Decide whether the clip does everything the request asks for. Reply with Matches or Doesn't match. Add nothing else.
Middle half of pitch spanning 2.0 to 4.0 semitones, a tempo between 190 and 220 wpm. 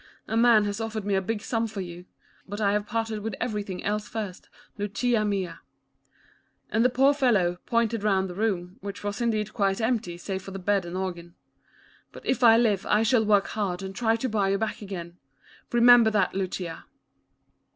Matches